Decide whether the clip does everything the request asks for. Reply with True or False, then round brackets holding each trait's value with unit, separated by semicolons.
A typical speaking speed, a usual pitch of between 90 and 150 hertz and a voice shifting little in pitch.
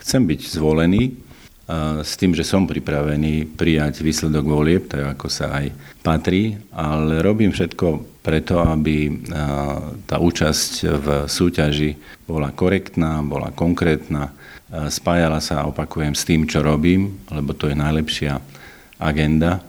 False (125 wpm; 80 Hz; 2.3 semitones)